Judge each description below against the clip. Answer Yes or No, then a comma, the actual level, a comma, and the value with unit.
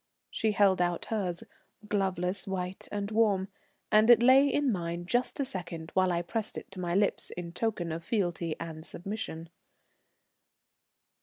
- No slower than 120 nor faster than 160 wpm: Yes, average, 155 wpm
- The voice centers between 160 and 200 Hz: Yes, high, 190 Hz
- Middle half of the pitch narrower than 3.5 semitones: No, average, 3.8 semitones